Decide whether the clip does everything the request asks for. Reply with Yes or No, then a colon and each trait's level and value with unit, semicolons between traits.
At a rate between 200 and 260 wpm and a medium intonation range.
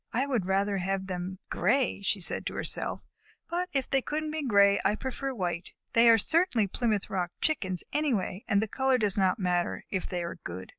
No: fast, 205 wpm; wide, 5.9 semitones